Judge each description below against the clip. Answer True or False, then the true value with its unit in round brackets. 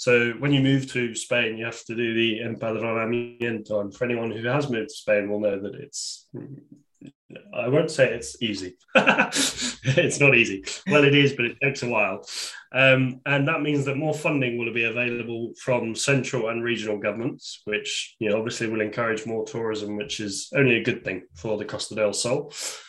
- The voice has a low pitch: True (115 Hz)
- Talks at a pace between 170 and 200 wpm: True (195 wpm)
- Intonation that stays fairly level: False (3.0 semitones)